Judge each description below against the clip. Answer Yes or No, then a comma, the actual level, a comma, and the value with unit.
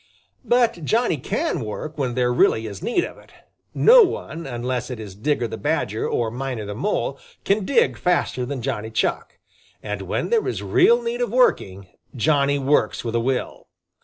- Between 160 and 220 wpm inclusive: Yes, average, 180 wpm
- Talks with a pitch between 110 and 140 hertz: Yes, low, 135 Hz